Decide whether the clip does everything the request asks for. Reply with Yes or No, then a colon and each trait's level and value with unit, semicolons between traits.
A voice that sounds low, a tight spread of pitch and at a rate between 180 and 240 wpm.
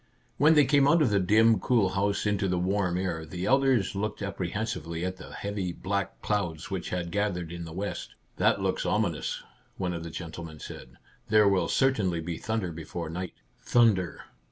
No: very low, 95 Hz; average, 3.5 semitones; average, 200 wpm